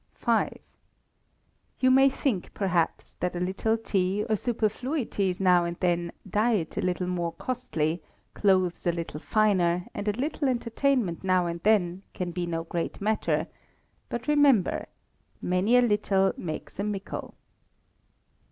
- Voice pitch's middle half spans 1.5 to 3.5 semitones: No, average, 4.3 semitones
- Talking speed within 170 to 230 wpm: No, average, 140 wpm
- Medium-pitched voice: No, high, 195 Hz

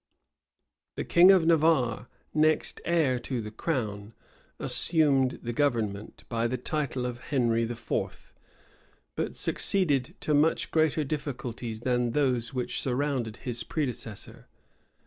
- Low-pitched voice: Yes, low, 130 Hz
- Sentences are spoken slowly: Yes, slow, 120 wpm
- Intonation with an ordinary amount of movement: Yes, average, 4.4 semitones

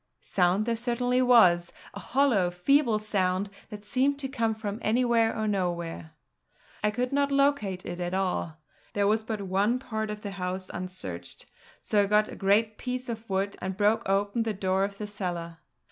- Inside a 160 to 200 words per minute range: Yes, average, 180 wpm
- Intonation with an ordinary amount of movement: Yes, average, 3.7 semitones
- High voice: Yes, high, 210 Hz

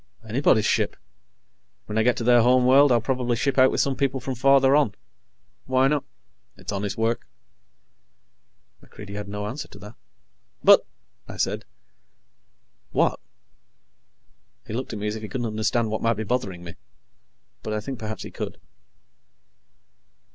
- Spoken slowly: No, average, 160 wpm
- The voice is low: Yes, low, 115 Hz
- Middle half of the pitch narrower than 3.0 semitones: No, average, 3.6 semitones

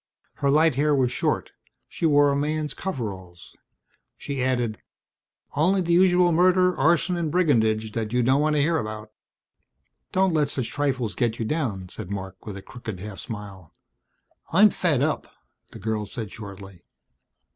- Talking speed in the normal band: Yes, average, 160 wpm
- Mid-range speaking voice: No, low, 130 Hz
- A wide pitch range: Yes, wide, 6.6 semitones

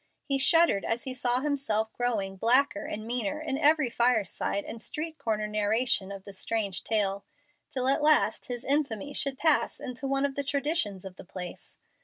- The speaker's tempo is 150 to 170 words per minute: No, average, 180 wpm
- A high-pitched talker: Yes, high, 245 Hz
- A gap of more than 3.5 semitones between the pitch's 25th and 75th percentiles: Yes, average, 5.1 semitones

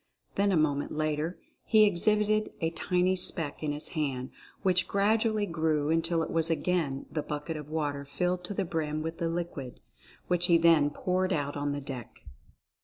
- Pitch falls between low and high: Yes, medium, 165 Hz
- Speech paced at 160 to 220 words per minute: Yes, average, 180 wpm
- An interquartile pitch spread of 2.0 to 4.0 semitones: Yes, average, 3.4 semitones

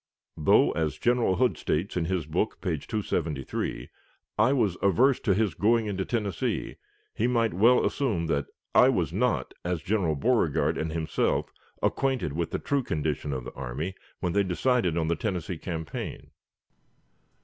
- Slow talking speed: No, average, 160 wpm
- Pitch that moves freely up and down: Yes, wide, 5.9 semitones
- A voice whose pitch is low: Yes, very low, 90 Hz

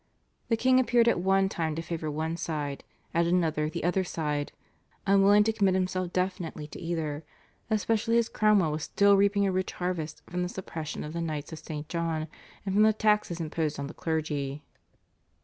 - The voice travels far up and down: No, average, 4.1 semitones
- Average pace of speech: Yes, average, 185 wpm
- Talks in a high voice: No, medium, 175 Hz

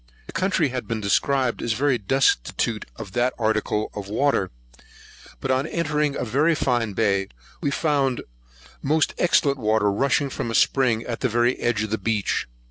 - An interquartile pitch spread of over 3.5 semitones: Yes, average, 4.2 semitones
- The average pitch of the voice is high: No, low, 120 Hz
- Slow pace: No, average, 170 wpm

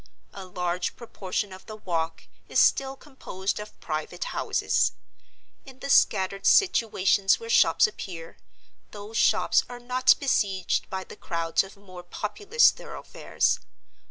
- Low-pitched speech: No, high, 195 Hz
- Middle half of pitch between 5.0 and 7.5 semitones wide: Yes, wide, 5.5 semitones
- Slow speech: Yes, slow, 130 wpm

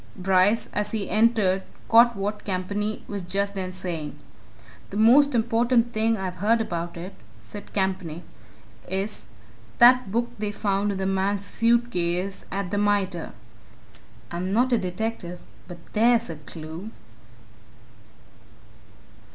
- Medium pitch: No, high, 200 Hz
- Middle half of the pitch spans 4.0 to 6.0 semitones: No, average, 3.4 semitones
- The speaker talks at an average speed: No, slow, 130 wpm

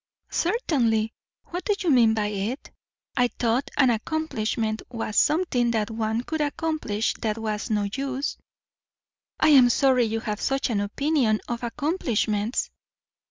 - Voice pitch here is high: Yes, high, 240 Hz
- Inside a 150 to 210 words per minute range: No, average, 140 wpm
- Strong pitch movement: No, average, 4.7 semitones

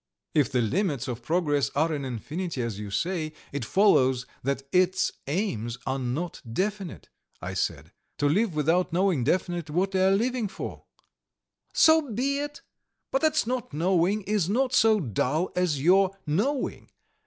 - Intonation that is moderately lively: No, wide, 6.5 semitones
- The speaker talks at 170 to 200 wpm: No, average, 155 wpm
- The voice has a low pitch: No, medium, 175 Hz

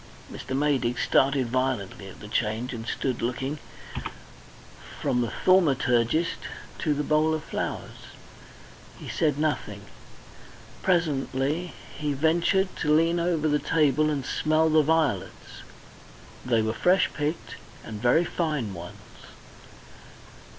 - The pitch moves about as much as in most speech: Yes, average, 4.4 semitones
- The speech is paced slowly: Yes, slow, 120 wpm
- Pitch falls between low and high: Yes, medium, 145 Hz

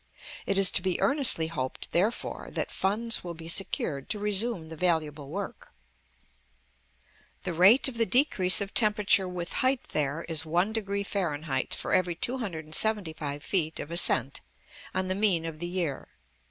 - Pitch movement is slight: No, average, 4.3 semitones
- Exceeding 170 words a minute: No, average, 155 wpm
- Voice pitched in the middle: Yes, medium, 180 Hz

